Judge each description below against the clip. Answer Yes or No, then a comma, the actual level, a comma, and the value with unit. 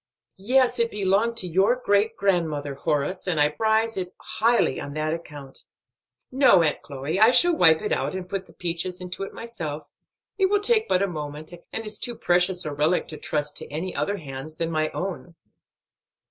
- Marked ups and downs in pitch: Yes, wide, 5.8 semitones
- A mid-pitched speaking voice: Yes, medium, 180 Hz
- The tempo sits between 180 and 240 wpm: Yes, average, 190 wpm